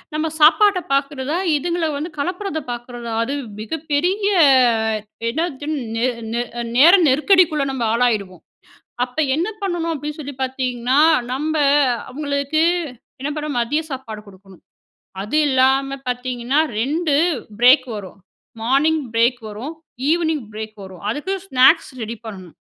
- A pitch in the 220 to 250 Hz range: No, very high, 275 Hz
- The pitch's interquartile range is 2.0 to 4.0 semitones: No, average, 4.7 semitones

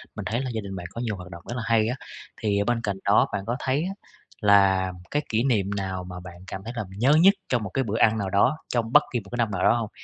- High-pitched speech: No, low, 110 Hz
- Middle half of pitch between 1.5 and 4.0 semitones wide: Yes, average, 3.7 semitones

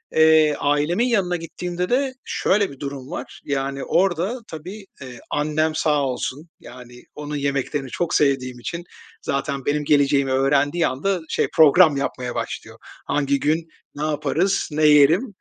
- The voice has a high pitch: No, medium, 150 Hz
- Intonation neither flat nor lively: Yes, average, 3.9 semitones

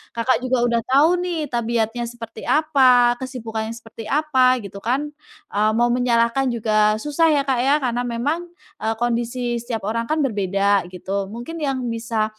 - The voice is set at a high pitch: Yes, high, 240 Hz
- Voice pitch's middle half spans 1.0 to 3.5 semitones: Yes, average, 2.8 semitones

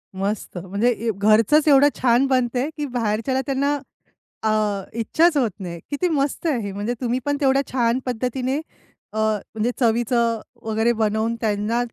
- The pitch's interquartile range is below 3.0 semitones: No, average, 3.6 semitones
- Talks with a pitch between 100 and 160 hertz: No, high, 235 Hz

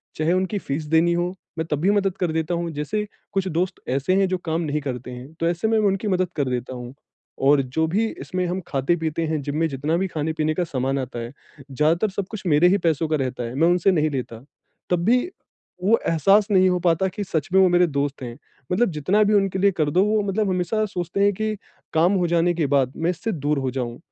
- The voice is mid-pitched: Yes, medium, 170 Hz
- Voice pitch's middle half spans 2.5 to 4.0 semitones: No, average, 4.5 semitones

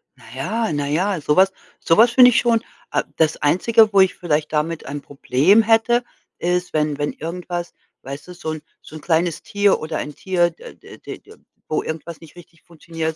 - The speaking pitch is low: No, medium, 170 Hz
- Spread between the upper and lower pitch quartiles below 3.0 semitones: No, average, 4.1 semitones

